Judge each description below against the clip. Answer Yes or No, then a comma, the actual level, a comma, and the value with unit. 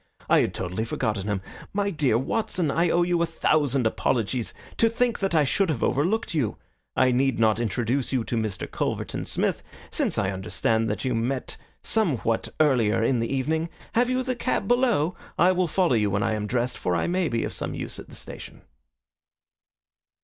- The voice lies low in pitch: Yes, low, 130 Hz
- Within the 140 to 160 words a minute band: No, average, 195 wpm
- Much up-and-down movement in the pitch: Yes, wide, 7.5 semitones